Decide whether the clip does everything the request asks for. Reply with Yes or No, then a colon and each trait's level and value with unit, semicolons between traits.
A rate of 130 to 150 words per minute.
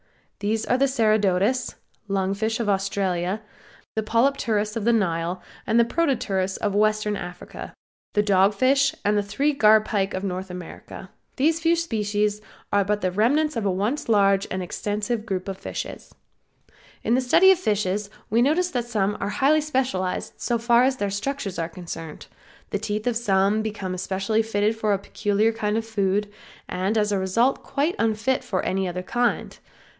No: average, 170 wpm